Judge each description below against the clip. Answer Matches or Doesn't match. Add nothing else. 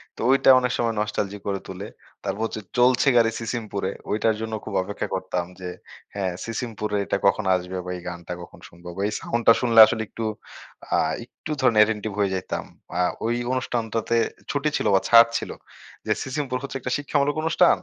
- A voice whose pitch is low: Matches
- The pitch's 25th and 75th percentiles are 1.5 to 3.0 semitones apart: Doesn't match